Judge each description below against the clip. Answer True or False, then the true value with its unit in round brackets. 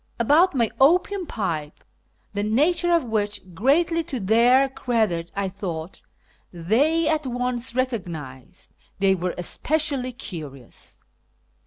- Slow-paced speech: True (115 wpm)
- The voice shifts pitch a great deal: True (7.3 semitones)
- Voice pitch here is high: True (235 Hz)